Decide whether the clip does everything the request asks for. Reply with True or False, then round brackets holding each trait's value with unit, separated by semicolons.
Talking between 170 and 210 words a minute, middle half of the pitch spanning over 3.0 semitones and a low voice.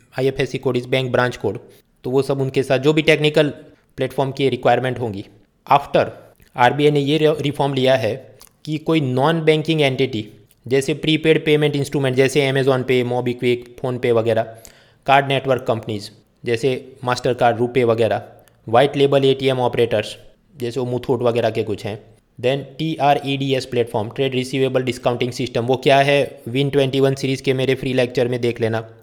False (175 wpm; 2.5 semitones; 130 Hz)